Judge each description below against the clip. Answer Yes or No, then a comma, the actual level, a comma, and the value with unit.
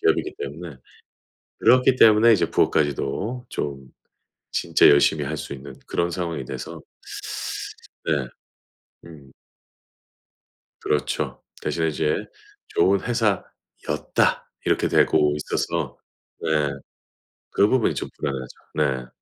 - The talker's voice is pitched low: Yes, very low, 80 Hz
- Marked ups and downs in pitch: Yes, wide, 6.1 semitones